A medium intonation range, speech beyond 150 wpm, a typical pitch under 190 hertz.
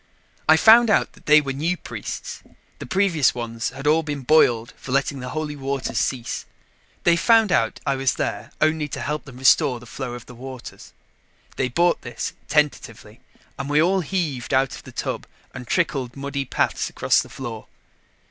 Yes: average, 3.8 semitones; average, 185 wpm; medium, 140 Hz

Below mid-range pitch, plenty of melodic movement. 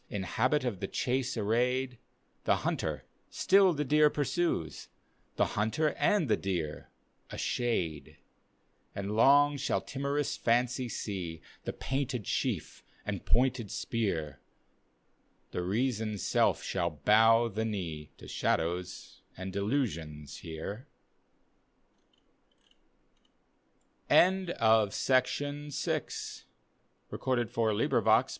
Yes: low, 110 Hz; wide, 6.0 semitones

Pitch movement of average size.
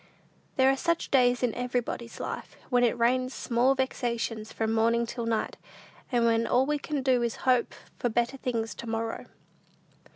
No: narrow, 1.9 semitones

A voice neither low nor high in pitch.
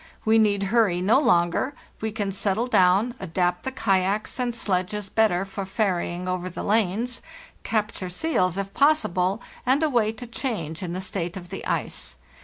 No: high, 195 Hz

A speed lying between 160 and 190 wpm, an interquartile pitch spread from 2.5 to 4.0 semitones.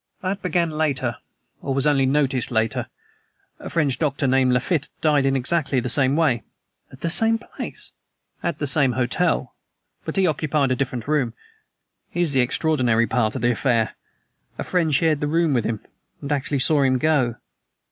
Yes: average, 175 wpm; average, 3.7 semitones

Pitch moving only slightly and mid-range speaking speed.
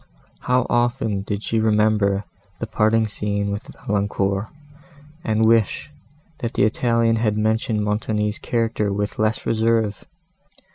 No: narrow, 1.6 semitones; slow, 125 wpm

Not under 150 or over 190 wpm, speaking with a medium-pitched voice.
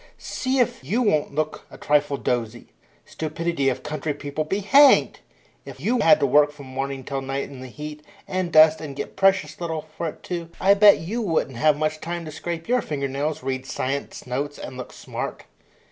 No: average, 200 wpm; medium, 150 Hz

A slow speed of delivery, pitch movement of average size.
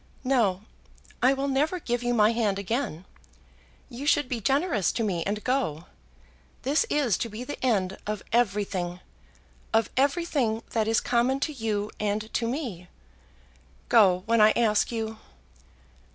No: average, 150 wpm; average, 4.0 semitones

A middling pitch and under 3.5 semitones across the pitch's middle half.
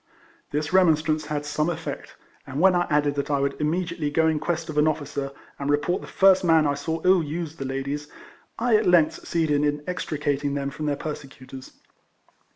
Yes: medium, 150 Hz; narrow, 2.4 semitones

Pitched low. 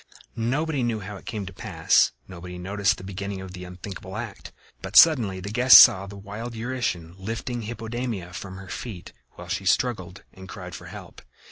Yes: low, 100 Hz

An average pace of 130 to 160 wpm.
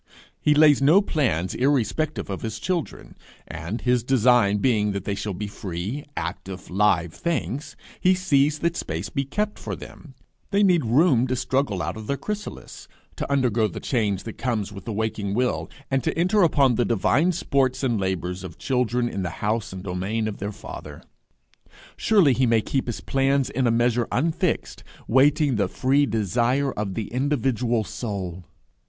No: average, 175 wpm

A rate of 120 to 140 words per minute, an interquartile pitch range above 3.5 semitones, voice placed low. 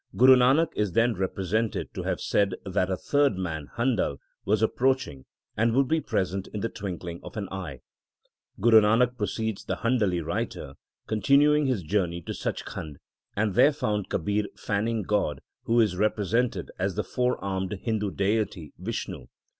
No: average, 160 wpm; average, 4.0 semitones; low, 105 Hz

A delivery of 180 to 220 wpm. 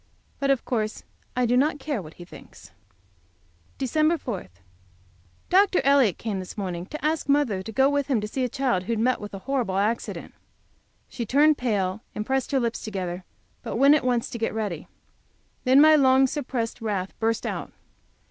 Yes: average, 185 wpm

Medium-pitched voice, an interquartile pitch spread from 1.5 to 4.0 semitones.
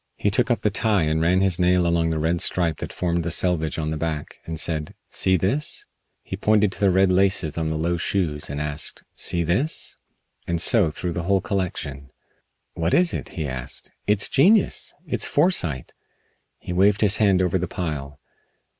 No: very low, 90 Hz; average, 3.6 semitones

